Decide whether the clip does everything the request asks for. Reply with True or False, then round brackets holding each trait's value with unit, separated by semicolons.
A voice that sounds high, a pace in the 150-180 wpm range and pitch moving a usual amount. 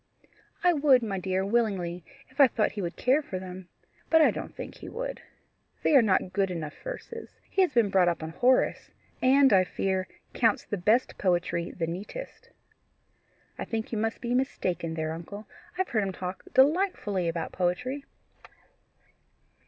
False (205 Hz; 175 wpm; 6.3 semitones)